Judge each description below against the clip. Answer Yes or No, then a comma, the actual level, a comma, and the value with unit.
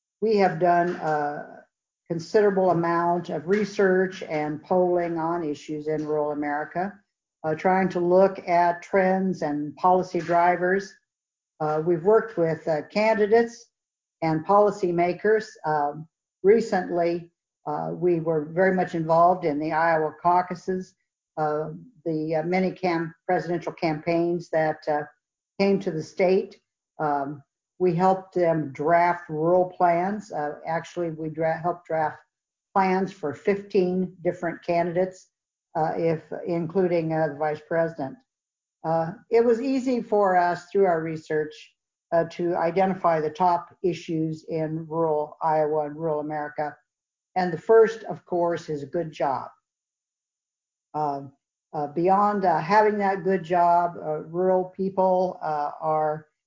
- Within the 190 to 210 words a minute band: No, slow, 135 wpm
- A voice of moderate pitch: Yes, medium, 170 Hz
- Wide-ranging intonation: No, average, 3.1 semitones